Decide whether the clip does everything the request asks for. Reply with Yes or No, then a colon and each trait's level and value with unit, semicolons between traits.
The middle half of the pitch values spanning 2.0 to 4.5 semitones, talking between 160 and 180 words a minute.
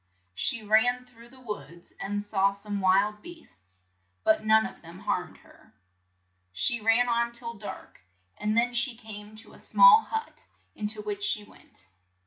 Yes: narrow, 2.5 semitones; average, 165 wpm